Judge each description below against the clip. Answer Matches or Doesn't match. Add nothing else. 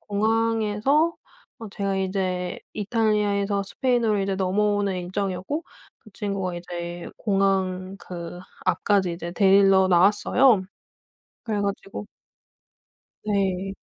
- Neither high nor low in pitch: Doesn't match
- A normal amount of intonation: Doesn't match